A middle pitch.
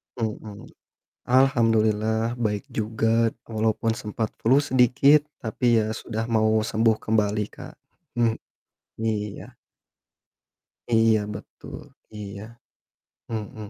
No: low, 110 Hz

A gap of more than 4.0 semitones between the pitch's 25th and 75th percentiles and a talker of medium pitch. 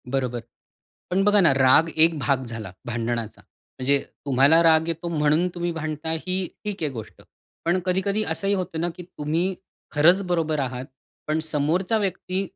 Yes: average, 4.5 semitones; medium, 160 Hz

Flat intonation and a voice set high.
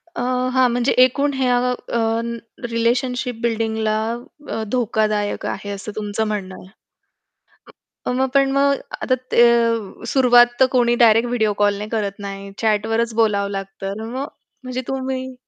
No: average, 3.1 semitones; high, 230 Hz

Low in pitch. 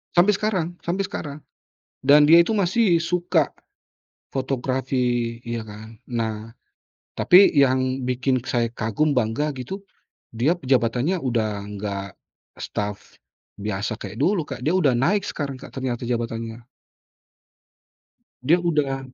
Yes: low, 130 Hz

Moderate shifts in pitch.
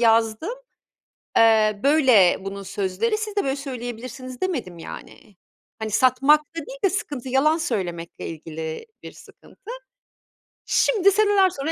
No: wide, 7.9 semitones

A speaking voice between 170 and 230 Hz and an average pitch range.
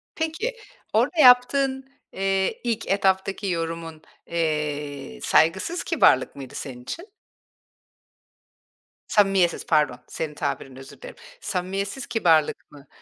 No: medium, 185 Hz; wide, 7.3 semitones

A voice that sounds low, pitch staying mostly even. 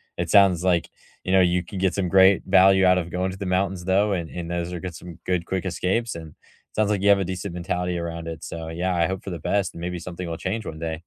Yes: very low, 90 Hz; narrow, 1.9 semitones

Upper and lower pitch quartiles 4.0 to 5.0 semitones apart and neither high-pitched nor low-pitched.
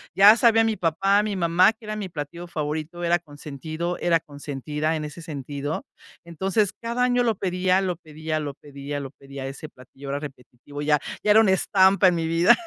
Yes: average, 4.6 semitones; medium, 165 Hz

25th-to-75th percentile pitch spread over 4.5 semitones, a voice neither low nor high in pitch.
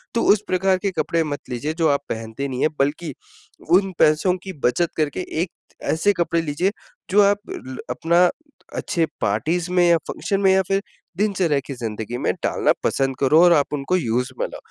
Yes: average, 5.1 semitones; medium, 165 Hz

